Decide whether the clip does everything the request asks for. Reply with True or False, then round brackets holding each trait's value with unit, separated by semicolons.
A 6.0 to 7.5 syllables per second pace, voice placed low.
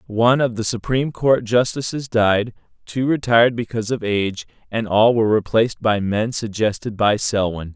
False (5.3 syllables/s; 110 Hz)